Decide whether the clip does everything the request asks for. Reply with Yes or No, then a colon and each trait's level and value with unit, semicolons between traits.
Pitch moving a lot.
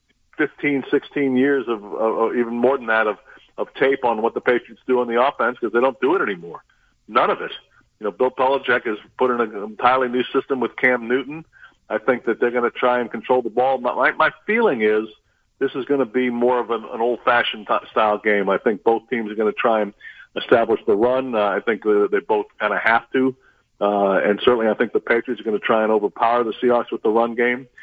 No: narrow, 2.6 semitones